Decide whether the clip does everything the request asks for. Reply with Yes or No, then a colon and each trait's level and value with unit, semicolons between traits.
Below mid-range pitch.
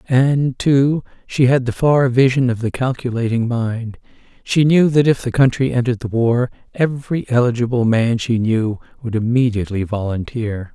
Yes: low, 120 Hz